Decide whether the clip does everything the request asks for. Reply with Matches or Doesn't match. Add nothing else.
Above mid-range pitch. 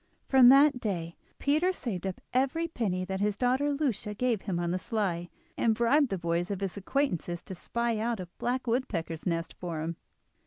Matches